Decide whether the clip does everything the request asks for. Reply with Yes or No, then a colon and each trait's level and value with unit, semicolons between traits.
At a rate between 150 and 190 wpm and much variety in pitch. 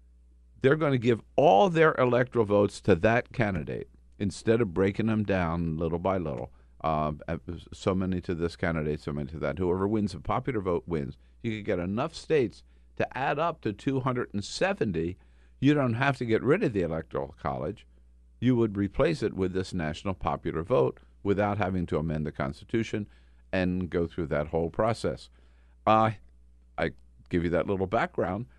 Yes: average, 175 wpm; wide, 7.4 semitones